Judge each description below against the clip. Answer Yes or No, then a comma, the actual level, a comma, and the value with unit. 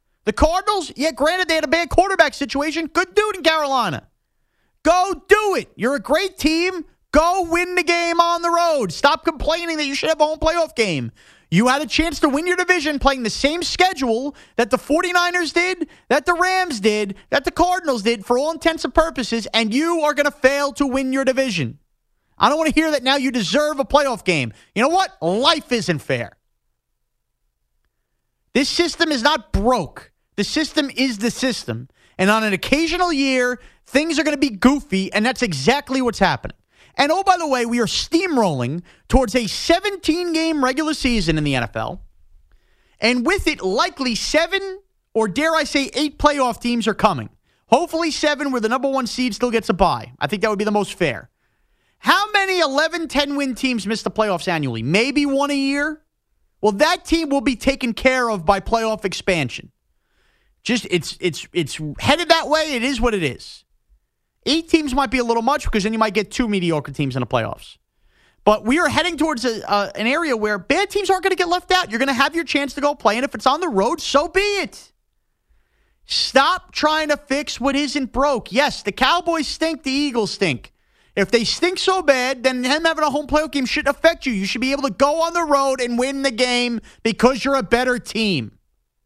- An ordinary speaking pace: No, fast, 210 wpm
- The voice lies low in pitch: No, very high, 275 Hz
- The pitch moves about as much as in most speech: No, wide, 6.2 semitones